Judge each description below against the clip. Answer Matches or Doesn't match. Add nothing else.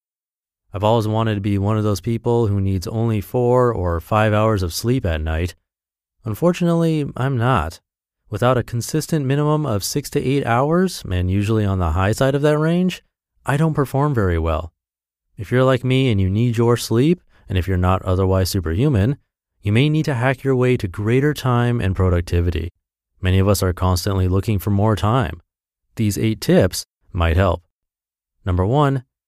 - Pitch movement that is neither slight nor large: Doesn't match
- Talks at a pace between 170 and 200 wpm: Matches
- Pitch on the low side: Matches